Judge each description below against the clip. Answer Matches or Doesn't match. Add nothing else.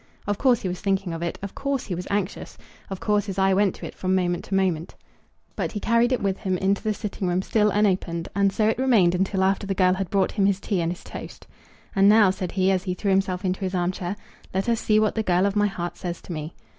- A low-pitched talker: Doesn't match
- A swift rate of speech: Matches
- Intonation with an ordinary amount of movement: Doesn't match